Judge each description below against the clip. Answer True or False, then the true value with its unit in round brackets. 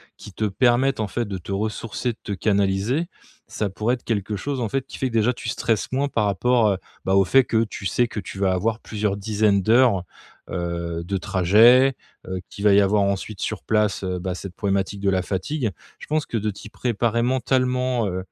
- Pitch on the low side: True (105 Hz)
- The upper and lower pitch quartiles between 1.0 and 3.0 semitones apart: False (3.8 semitones)